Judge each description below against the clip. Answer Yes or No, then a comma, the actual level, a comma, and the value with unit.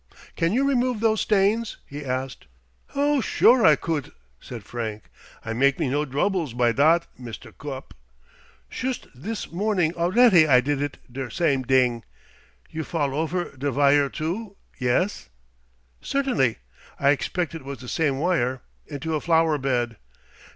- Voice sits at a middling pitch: Yes, medium, 150 Hz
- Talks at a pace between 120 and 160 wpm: Yes, average, 150 wpm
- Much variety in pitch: Yes, wide, 5.8 semitones